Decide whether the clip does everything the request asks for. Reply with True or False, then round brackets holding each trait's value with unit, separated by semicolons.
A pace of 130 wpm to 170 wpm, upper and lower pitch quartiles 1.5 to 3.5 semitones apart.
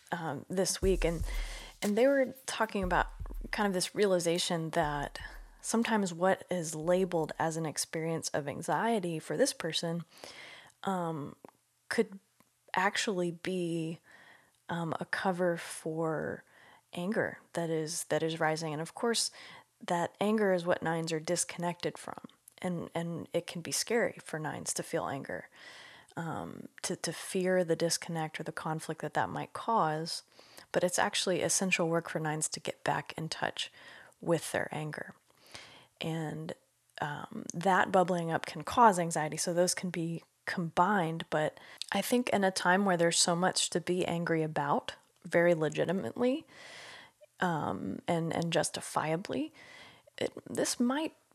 True (145 wpm; 2.8 semitones)